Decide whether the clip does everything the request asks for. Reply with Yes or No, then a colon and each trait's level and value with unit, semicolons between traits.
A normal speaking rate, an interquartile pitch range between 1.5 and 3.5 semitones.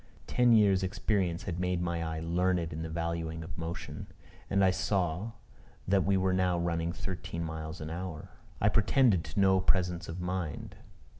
Yes: average, 170 wpm; narrow, 2.4 semitones